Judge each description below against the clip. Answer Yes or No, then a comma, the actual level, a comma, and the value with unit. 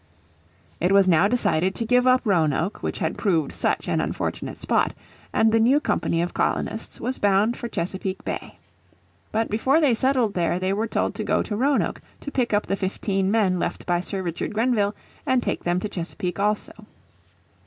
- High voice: Yes, high, 205 Hz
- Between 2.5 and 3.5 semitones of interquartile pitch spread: No, average, 4.0 semitones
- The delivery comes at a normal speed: Yes, average, 185 wpm